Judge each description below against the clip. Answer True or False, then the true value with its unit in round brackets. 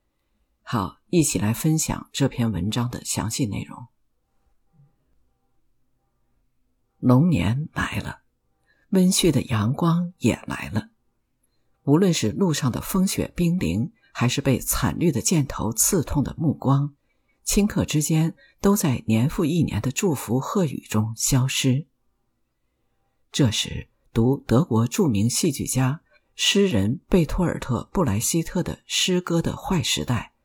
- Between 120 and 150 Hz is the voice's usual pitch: True (135 Hz)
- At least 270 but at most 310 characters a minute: False (185 characters per minute)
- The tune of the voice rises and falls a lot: True (6.9 semitones)